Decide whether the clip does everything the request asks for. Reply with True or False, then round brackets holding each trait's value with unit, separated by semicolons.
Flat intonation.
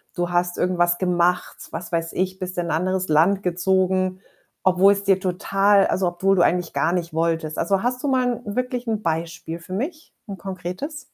True (2.2 semitones)